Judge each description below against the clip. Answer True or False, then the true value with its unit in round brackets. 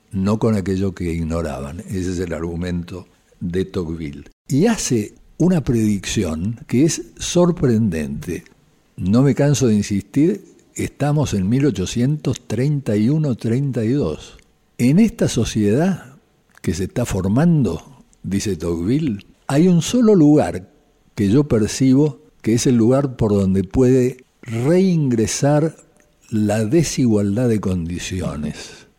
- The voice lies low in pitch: True (115 Hz)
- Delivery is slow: True (110 wpm)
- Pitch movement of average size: False (6.7 semitones)